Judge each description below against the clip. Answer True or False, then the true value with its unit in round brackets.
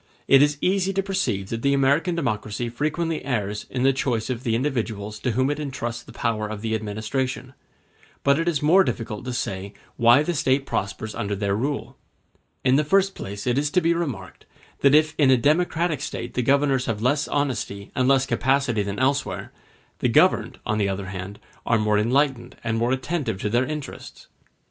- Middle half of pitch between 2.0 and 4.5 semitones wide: False (5.0 semitones)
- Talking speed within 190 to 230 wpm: True (195 wpm)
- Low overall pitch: True (130 Hz)